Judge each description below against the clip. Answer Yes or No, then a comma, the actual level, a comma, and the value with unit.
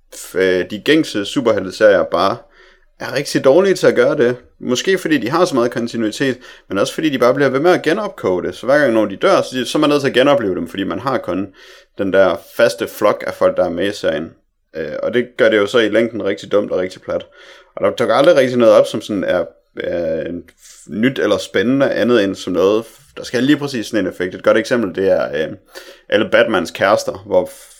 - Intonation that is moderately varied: No, wide, 7.1 semitones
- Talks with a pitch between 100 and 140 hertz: Yes, low, 135 Hz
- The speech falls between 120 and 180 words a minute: No, fast, 225 wpm